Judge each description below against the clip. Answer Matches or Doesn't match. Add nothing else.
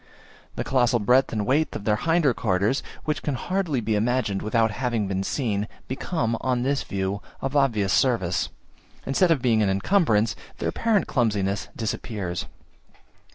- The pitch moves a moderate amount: Matches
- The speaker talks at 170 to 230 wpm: Doesn't match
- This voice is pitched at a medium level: Doesn't match